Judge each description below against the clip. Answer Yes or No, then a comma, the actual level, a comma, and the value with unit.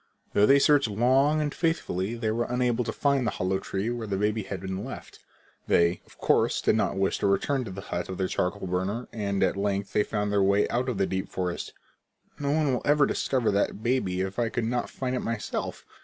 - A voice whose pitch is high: No, low, 105 Hz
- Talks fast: Yes, fast, 230 wpm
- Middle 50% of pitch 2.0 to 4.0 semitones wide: No, average, 4.5 semitones